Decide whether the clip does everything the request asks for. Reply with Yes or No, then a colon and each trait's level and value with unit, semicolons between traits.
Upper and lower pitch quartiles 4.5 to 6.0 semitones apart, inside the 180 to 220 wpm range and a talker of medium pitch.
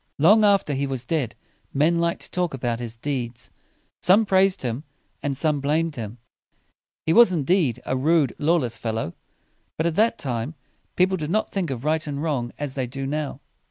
Yes: average, 4.8 semitones; average, 185 wpm; medium, 145 Hz